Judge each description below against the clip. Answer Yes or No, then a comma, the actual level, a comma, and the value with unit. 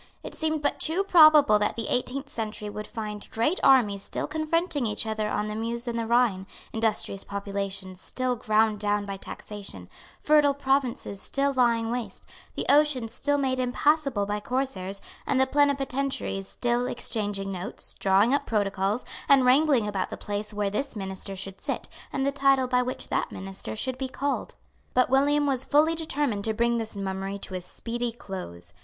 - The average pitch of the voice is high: Yes, high, 235 Hz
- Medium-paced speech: Yes, average, 175 wpm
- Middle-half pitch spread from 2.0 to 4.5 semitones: No, average, 5.1 semitones